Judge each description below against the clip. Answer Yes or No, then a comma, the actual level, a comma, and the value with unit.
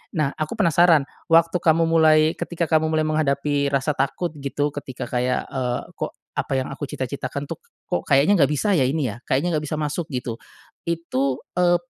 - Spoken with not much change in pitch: No, average, 3.1 semitones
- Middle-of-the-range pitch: Yes, medium, 150 Hz